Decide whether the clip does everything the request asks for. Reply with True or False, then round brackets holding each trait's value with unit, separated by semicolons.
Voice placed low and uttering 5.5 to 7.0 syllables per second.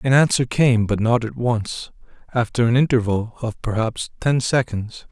False (120 Hz; 4.5 syllables/s)